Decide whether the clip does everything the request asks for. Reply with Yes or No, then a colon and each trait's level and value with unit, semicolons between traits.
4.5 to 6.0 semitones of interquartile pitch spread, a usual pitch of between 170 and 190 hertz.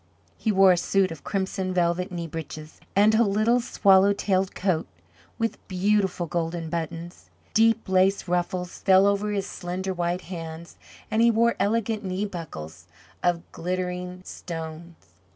No: average, 2.8 semitones; medium, 185 Hz